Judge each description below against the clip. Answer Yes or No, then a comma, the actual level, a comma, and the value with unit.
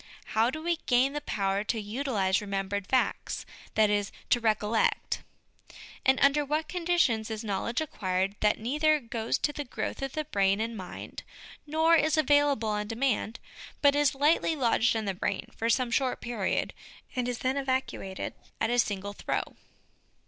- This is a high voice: Yes, high, 240 Hz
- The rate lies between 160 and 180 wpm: Yes, average, 170 wpm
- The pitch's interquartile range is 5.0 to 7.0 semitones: Yes, wide, 5.4 semitones